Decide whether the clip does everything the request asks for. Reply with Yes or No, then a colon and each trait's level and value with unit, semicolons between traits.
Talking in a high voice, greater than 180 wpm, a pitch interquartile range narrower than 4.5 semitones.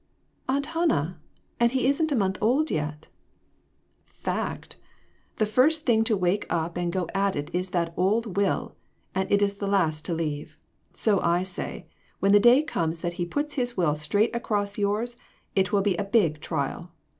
No: high, 200 Hz; average, 190 wpm; average, 5.2 semitones